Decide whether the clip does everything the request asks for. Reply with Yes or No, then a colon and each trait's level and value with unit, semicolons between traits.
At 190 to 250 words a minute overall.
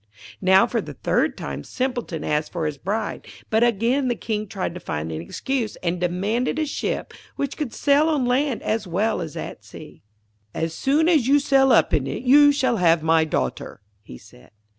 Yes: average, 195 wpm